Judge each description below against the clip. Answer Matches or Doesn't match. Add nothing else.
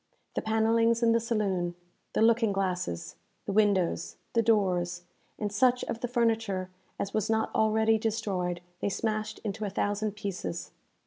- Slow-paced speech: Doesn't match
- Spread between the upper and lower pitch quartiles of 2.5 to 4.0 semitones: Matches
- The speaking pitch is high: Matches